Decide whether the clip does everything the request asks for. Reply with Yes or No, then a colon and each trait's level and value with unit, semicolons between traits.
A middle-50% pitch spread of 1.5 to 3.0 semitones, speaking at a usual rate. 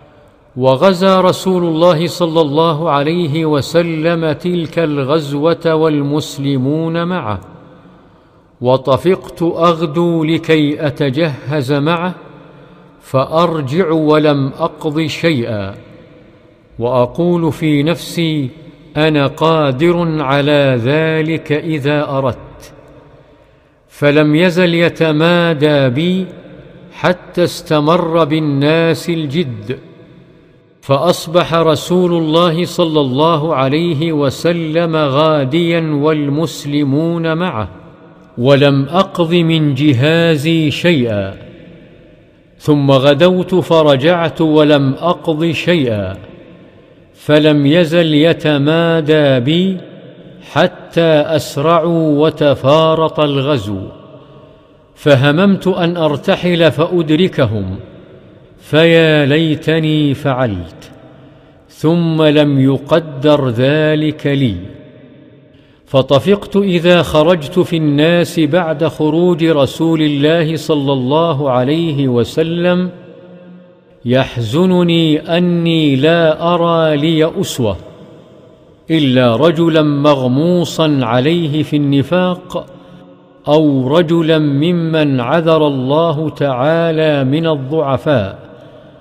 No: narrow, 2.4 semitones; slow, 75 wpm